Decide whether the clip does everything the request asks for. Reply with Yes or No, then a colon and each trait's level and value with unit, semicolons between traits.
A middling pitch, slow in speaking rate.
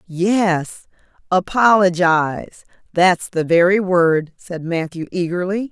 Yes: medium, 180 Hz; slow, 75 wpm